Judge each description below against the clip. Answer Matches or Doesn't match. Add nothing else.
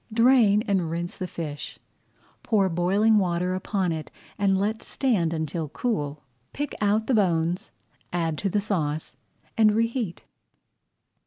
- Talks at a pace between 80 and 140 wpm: Matches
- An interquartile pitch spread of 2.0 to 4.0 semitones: Doesn't match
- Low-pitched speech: Doesn't match